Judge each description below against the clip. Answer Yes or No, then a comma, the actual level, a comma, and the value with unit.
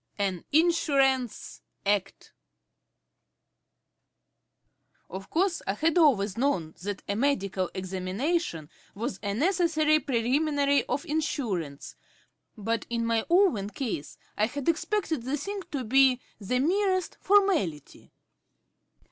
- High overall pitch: Yes, very high, 260 Hz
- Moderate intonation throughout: No, wide, 7.8 semitones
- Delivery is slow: Yes, slow, 105 wpm